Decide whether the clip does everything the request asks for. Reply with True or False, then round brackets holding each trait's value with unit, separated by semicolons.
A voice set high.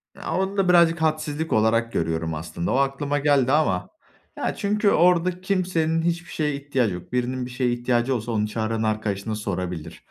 False (130 Hz)